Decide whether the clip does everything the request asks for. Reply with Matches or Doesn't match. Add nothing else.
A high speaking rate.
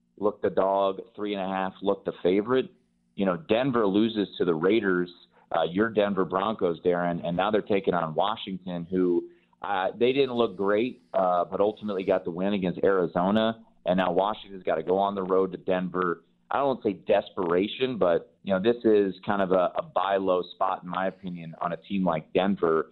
Doesn't match